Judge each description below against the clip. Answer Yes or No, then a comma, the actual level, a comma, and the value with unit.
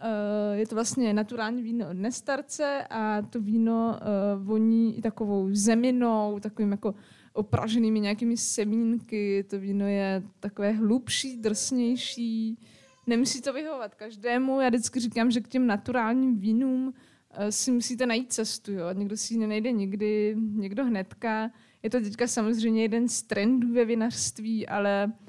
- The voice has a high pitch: Yes, high, 225 Hz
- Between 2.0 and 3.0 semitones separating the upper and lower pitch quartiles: Yes, narrow, 2.4 semitones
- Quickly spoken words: No, average, 140 wpm